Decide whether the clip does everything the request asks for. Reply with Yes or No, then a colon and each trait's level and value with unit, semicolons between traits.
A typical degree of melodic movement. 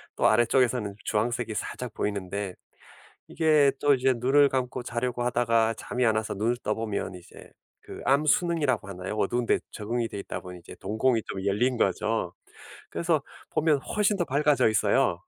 Yes: average, 4.1 semitones